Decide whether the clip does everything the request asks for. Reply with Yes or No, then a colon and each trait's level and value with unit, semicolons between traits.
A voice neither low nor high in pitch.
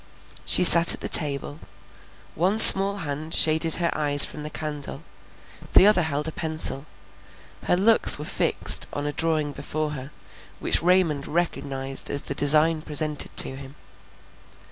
Yes: medium, 155 Hz